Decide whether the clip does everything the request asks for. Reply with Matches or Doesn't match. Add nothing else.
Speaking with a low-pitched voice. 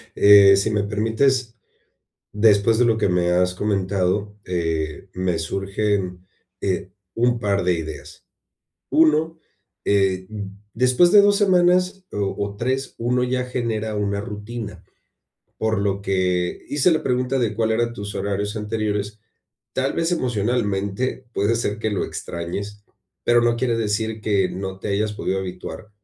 Matches